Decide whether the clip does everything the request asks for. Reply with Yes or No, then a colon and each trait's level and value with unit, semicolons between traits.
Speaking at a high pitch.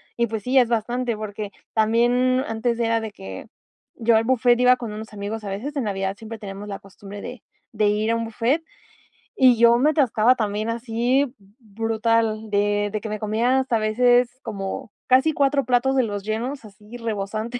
Yes: high, 225 Hz